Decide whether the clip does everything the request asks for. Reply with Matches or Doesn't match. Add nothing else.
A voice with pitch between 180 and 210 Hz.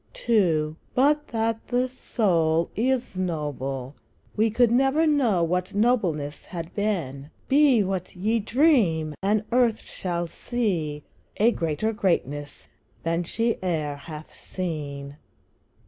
Matches